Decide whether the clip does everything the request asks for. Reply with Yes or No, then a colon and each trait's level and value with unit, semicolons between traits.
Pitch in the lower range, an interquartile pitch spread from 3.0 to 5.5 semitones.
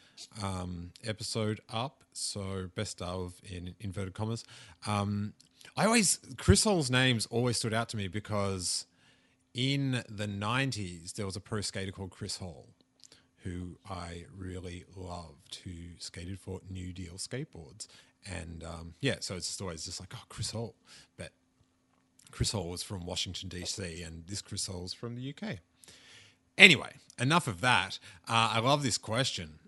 Yes: low, 100 Hz; average, 4.2 semitones